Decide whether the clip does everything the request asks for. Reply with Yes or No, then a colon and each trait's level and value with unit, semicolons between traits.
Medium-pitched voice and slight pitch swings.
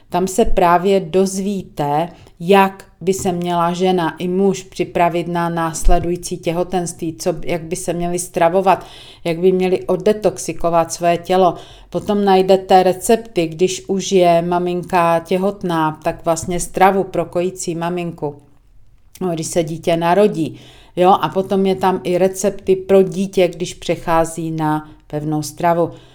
Yes: medium, 175 Hz; narrow, 1.9 semitones